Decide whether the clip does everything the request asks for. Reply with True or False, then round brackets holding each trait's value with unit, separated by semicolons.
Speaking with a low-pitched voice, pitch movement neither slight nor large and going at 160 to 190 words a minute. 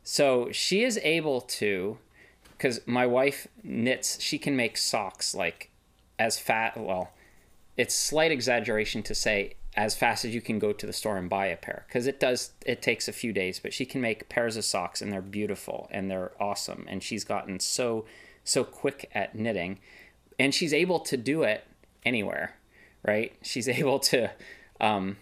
True (110 Hz; 4.1 semitones; 180 wpm)